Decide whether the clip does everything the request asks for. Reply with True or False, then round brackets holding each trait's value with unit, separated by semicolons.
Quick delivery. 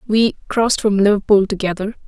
False (145 wpm)